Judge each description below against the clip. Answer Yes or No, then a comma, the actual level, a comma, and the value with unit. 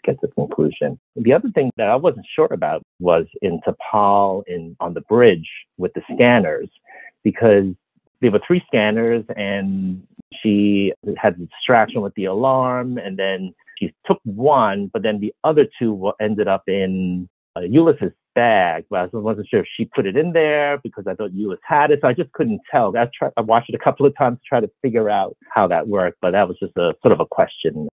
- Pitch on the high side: No, low, 105 Hz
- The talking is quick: Yes, fast, 210 wpm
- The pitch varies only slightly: No, average, 4.8 semitones